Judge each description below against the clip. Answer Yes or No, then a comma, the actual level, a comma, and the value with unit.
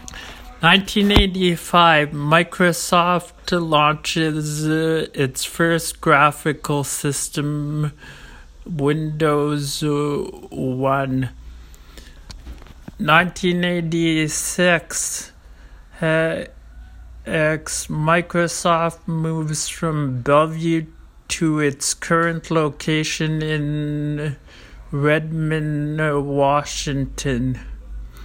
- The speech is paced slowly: Yes, slow, 45 wpm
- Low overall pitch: No, medium, 150 Hz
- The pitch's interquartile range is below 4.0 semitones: Yes, average, 3.2 semitones